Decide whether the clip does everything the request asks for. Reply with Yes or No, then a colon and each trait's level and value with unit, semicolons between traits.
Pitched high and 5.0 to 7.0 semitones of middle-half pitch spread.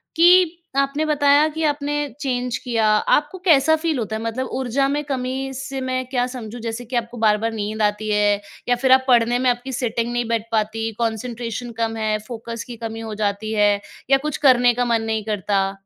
No: high, 240 Hz; average, 3.3 semitones